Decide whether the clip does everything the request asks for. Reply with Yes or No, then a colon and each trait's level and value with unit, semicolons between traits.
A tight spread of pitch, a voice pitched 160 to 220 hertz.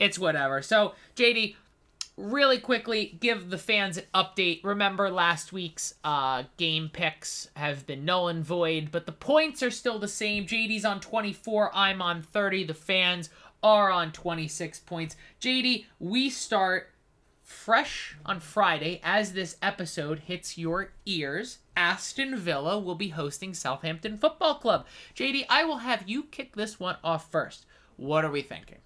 No: average, 4.7 semitones; high, 190 Hz